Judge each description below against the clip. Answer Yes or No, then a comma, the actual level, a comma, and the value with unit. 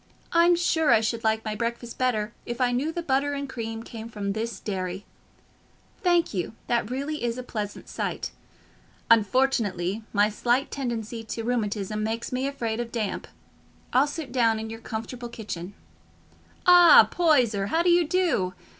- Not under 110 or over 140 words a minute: No, average, 165 wpm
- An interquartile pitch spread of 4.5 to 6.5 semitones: No, average, 3.9 semitones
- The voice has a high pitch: Yes, high, 235 Hz